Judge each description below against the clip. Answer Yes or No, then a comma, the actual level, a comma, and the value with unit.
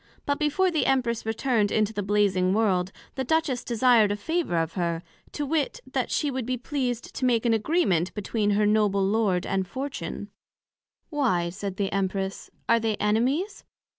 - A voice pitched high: Yes, high, 220 Hz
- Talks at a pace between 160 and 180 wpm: Yes, average, 170 wpm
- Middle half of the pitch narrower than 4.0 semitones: No, average, 5.1 semitones